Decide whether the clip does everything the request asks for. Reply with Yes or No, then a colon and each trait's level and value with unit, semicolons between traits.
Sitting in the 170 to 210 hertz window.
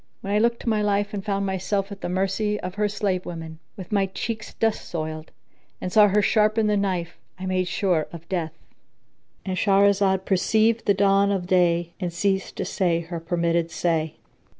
Yes: high, 190 Hz